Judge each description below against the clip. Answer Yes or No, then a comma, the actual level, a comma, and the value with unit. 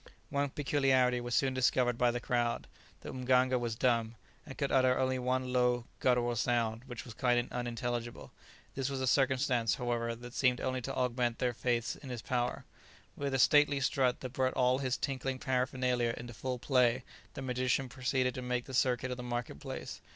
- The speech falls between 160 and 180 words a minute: No, average, 190 wpm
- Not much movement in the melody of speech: Yes, narrow, 1.2 semitones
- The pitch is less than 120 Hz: No, low, 125 Hz